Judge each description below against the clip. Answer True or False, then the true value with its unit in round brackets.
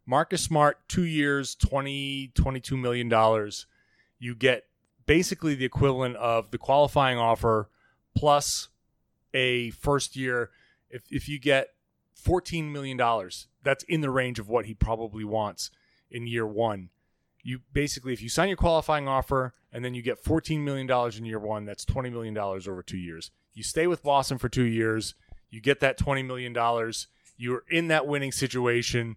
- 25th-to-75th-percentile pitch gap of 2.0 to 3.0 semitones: False (3.7 semitones)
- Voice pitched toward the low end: True (125 Hz)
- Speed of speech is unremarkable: True (170 wpm)